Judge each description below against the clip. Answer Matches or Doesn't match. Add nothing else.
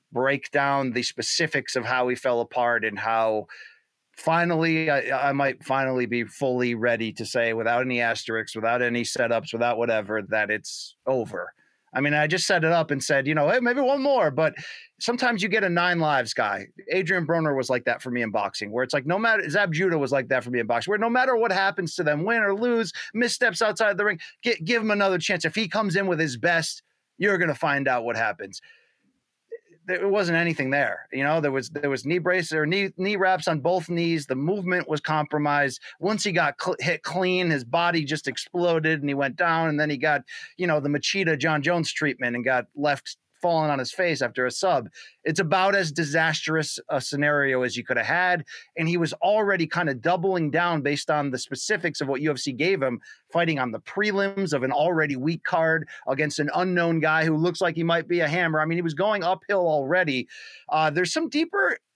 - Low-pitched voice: Doesn't match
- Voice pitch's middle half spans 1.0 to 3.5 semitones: Doesn't match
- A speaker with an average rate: Doesn't match